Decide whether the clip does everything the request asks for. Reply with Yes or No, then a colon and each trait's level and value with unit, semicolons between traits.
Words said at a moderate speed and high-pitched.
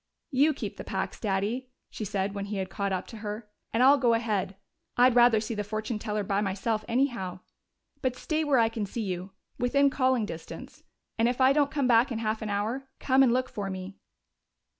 No: fast, 210 wpm; high, 225 Hz